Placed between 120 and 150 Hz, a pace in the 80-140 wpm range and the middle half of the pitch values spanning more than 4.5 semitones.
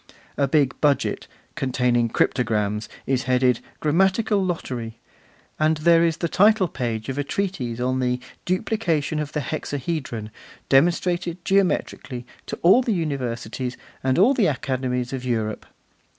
Yes: medium, 140 Hz; slow, 135 wpm; wide, 5.6 semitones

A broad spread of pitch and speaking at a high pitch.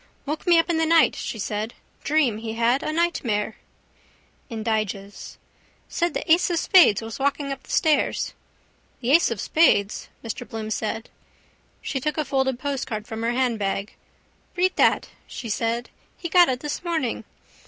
Yes: wide, 6.1 semitones; very high, 255 Hz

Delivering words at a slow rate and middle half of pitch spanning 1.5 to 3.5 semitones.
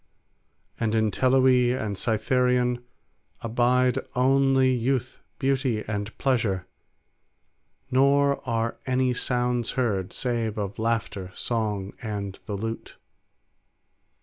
Yes: slow, 95 wpm; average, 2.9 semitones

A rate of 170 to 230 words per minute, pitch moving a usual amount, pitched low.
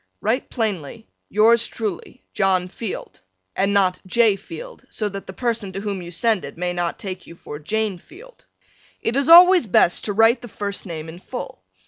No: average, 185 wpm; average, 4.2 semitones; high, 205 Hz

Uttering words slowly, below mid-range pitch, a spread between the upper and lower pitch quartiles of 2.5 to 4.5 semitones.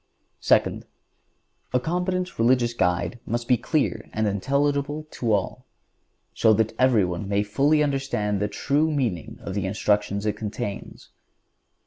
No: slow, 125 wpm; low, 115 Hz; average, 5.3 semitones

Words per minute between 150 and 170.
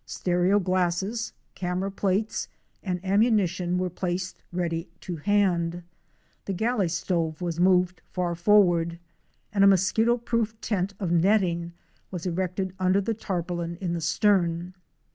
No: slow, 135 wpm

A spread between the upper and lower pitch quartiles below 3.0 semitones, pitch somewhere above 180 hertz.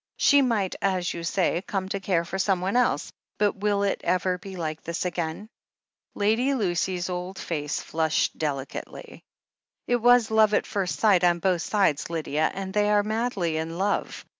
No: average, 3.5 semitones; high, 190 Hz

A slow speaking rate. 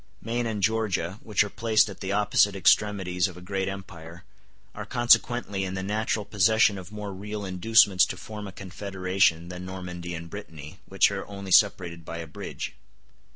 No: average, 175 wpm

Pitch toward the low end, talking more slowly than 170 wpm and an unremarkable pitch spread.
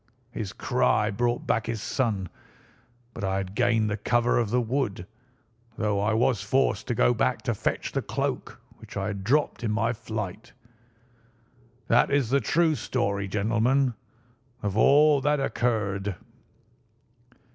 Yes: low, 115 Hz; average, 145 wpm; average, 3.4 semitones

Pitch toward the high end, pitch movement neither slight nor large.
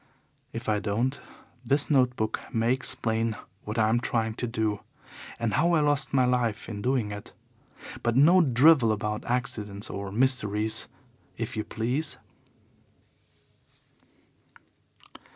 No: low, 115 Hz; average, 3.3 semitones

